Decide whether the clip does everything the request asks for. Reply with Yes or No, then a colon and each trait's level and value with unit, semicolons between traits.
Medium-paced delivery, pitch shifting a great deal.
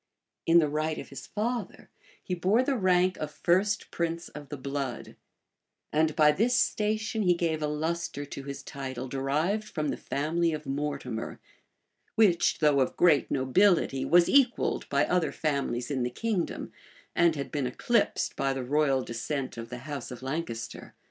No: average, 170 wpm; average, 4.5 semitones